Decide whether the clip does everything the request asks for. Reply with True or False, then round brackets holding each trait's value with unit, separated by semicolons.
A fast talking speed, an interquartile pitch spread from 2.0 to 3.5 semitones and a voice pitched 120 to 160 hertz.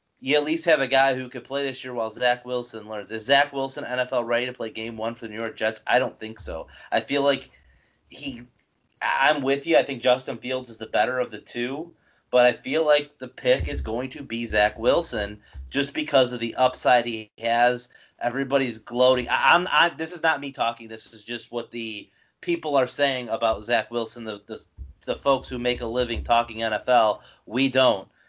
True (220 wpm; 3.1 semitones; 125 Hz)